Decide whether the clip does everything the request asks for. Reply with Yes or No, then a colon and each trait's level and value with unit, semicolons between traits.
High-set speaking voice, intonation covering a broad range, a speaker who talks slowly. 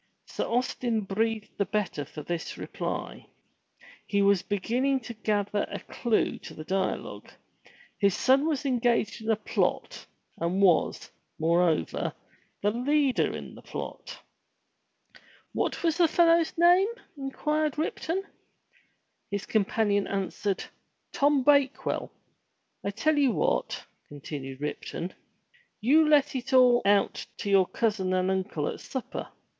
Yes: high, 220 Hz; wide, 6.1 semitones; slow, 130 wpm